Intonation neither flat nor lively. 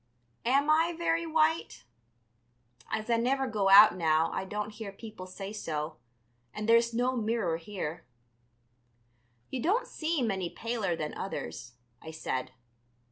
No: wide, 6.2 semitones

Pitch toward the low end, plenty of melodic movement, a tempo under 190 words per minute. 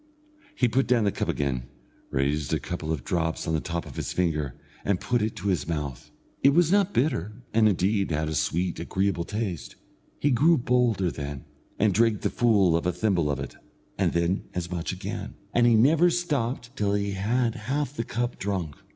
No: low, 100 Hz; wide, 6.5 semitones; average, 200 wpm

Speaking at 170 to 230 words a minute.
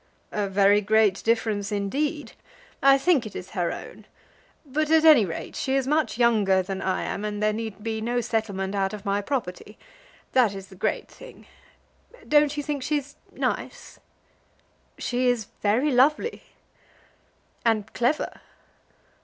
No: average, 150 wpm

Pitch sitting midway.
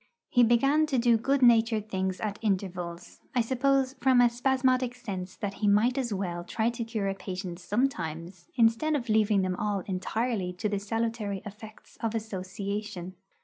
No: high, 215 Hz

